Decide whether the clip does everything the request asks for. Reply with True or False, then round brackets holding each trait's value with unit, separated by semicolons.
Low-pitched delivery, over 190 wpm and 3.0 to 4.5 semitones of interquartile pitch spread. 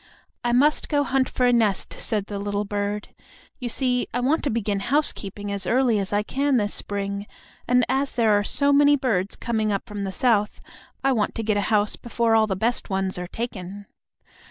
False (220 Hz; 205 wpm; 3.6 semitones)